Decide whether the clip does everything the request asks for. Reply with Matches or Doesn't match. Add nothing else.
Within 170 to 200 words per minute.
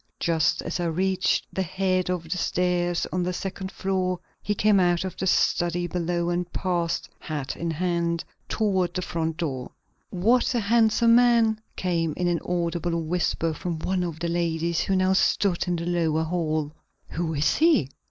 Matches